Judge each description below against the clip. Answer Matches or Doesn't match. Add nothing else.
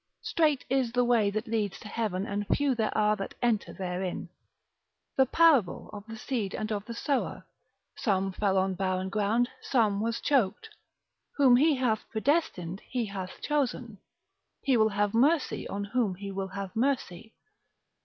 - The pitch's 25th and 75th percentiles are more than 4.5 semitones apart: Doesn't match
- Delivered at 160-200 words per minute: Matches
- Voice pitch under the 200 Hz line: Doesn't match